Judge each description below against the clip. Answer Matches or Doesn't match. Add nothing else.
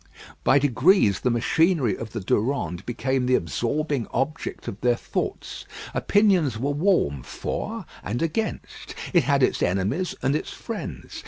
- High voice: Doesn't match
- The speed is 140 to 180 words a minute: Matches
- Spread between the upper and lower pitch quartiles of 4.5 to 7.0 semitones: Matches